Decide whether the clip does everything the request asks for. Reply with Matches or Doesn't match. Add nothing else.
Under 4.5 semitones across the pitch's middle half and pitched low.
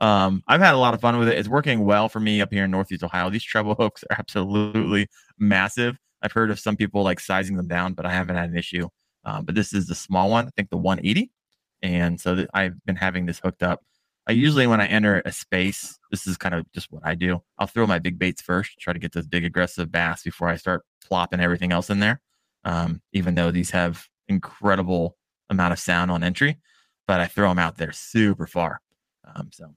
Matches